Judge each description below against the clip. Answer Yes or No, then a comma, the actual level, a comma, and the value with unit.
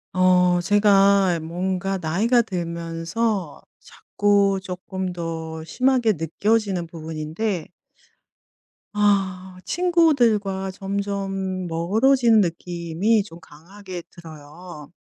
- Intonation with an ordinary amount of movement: Yes, average, 3.4 semitones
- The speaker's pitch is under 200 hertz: Yes, high, 190 Hz